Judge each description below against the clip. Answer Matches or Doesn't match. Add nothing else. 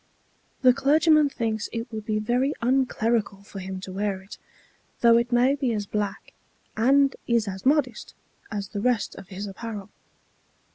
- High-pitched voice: Matches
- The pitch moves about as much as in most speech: Matches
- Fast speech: Doesn't match